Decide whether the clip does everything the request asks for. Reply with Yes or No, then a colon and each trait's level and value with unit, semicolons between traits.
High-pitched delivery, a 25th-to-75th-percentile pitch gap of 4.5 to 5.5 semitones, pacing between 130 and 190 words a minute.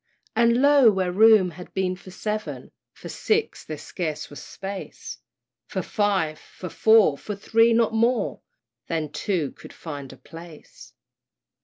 Yes: high, 195 Hz; average, 5.2 semitones; average, 145 wpm